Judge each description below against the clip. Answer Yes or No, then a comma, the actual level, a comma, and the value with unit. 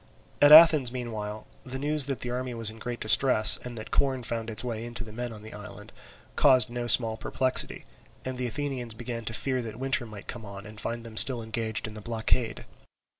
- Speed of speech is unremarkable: No, fast, 220 wpm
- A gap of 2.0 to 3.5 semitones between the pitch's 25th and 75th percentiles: Yes, narrow, 2.6 semitones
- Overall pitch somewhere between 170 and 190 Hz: No, low, 120 Hz